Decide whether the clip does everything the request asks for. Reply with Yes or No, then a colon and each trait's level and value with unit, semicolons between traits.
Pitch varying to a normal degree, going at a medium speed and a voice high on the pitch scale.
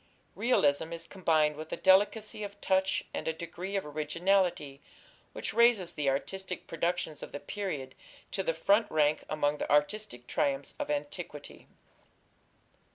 No: average, 4.6 semitones; average, 145 wpm; medium, 165 Hz